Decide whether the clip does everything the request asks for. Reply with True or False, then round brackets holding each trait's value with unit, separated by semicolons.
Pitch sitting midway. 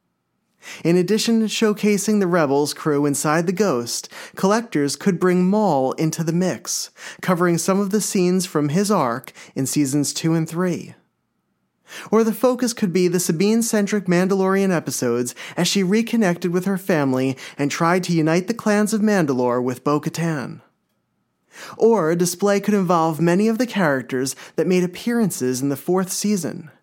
True (180 Hz)